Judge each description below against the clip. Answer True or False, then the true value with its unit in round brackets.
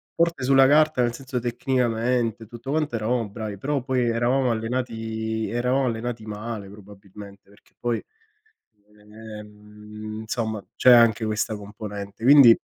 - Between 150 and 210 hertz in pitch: False (115 Hz)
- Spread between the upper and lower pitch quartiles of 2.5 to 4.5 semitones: True (2.8 semitones)